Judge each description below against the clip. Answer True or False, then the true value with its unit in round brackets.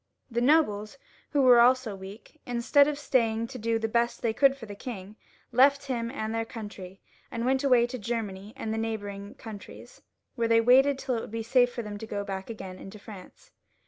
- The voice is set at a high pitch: True (230 Hz)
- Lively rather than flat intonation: False (3.3 semitones)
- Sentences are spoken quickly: True (210 wpm)